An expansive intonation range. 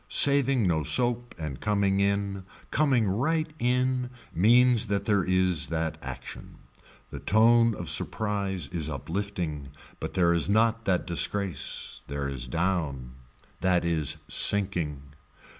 Yes: wide, 5.8 semitones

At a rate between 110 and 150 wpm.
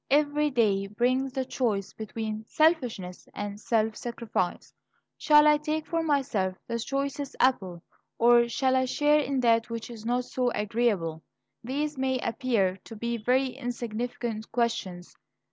Yes: average, 145 wpm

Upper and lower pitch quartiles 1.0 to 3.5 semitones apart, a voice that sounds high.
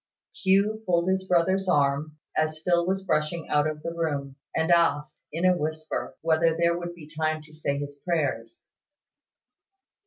No: narrow, 2.4 semitones; medium, 160 Hz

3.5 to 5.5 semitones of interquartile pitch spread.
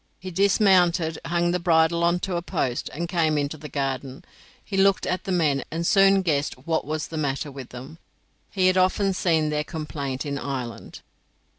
Yes: average, 4.2 semitones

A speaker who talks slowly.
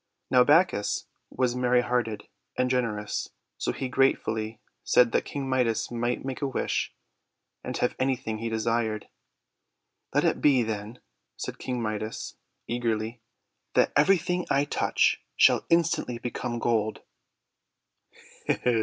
Yes: slow, 130 wpm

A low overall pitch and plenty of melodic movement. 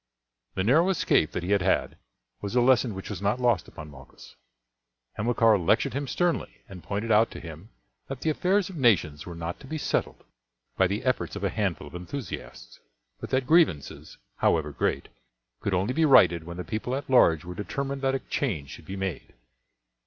Yes: low, 105 Hz; wide, 7.2 semitones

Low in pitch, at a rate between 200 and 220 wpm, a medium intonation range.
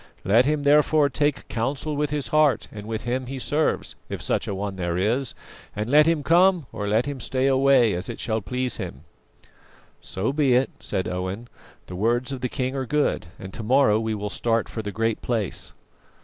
Yes: low, 125 Hz; fast, 205 wpm; average, 4.9 semitones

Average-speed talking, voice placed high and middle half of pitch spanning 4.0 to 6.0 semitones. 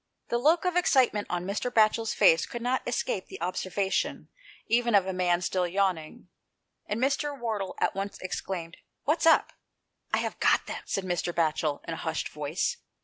Yes: average, 190 wpm; high, 195 Hz; wide, 5.5 semitones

